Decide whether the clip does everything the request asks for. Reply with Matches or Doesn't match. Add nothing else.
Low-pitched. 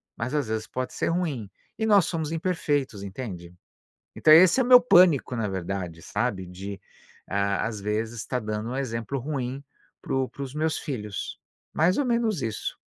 Matches